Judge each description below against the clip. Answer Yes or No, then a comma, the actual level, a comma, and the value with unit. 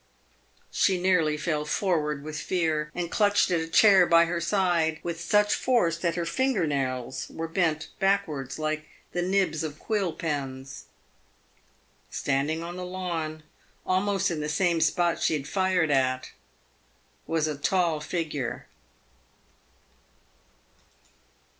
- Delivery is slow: Yes, slow, 130 wpm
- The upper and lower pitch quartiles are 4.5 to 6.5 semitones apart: No, average, 3.2 semitones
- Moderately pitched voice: Yes, medium, 165 Hz